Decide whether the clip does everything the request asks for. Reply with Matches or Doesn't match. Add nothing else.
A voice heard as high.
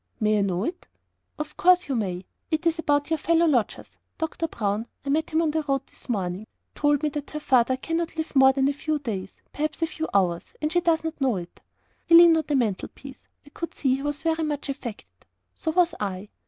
Matches